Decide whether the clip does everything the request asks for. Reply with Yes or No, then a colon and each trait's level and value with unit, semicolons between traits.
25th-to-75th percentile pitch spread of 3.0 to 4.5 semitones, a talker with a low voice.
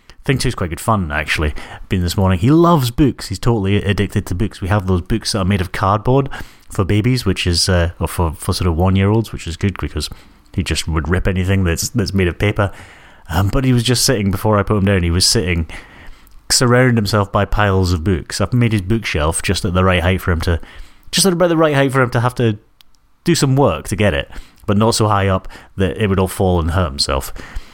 Yes: average, 3.8 semitones; low, 100 Hz